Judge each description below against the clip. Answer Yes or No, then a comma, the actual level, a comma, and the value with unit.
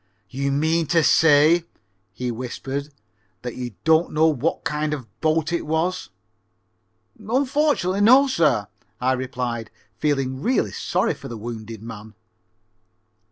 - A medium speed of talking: No, slow, 130 wpm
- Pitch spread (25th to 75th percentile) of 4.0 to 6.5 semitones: Yes, average, 5.0 semitones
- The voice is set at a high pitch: No, medium, 150 Hz